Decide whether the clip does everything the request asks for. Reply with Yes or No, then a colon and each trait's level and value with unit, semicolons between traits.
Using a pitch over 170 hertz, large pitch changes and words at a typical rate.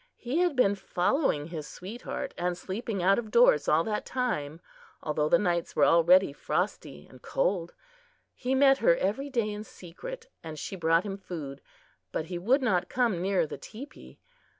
Yes: high, 190 Hz; wide, 6.7 semitones; average, 175 wpm